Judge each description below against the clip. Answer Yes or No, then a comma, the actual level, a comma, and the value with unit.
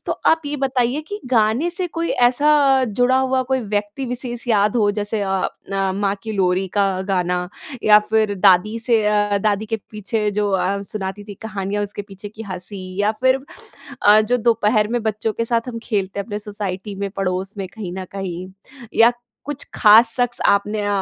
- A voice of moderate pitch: No, high, 210 Hz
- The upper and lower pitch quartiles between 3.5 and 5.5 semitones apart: No, average, 2.7 semitones